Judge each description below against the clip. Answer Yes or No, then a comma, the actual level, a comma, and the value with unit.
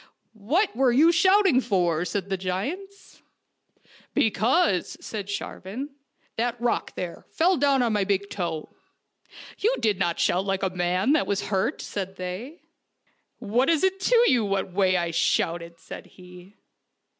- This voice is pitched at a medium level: No, high, 205 Hz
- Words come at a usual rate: Yes, average, 165 wpm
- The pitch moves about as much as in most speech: No, wide, 7.0 semitones